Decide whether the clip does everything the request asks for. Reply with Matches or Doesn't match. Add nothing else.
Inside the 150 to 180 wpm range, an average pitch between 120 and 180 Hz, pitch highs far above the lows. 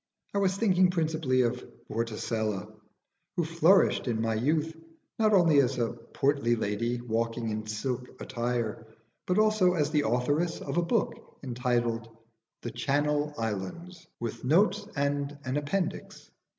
Doesn't match